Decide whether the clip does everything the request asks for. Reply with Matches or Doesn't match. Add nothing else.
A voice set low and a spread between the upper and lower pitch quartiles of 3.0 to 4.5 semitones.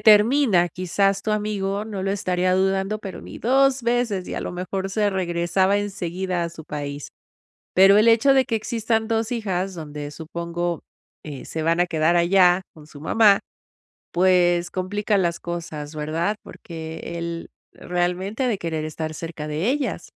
Doesn't match